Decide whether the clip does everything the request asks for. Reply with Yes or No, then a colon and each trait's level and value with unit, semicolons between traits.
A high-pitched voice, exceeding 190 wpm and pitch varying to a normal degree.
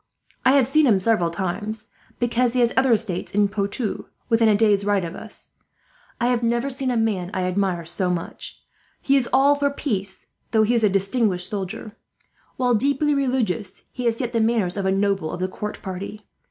Yes: high, 215 Hz; average, 200 wpm; average, 4.0 semitones